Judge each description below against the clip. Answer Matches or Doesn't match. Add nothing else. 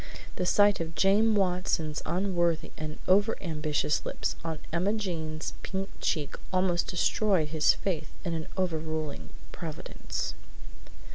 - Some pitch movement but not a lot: Matches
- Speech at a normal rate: Doesn't match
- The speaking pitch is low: Doesn't match